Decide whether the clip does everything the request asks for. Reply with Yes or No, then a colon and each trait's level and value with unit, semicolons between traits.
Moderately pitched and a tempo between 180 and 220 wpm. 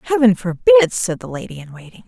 Yes: medium, 180 Hz; average, 200 wpm